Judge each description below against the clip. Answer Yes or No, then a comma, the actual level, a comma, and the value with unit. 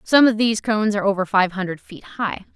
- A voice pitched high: Yes, high, 205 Hz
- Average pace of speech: No, fast, 235 wpm